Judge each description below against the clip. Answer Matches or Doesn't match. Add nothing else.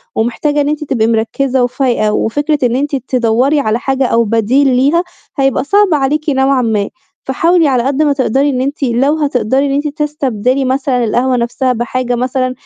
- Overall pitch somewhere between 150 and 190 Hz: Doesn't match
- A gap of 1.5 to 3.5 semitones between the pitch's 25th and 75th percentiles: Matches